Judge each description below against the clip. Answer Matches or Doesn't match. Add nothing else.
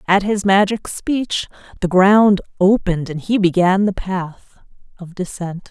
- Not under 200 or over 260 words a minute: Doesn't match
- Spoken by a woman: Matches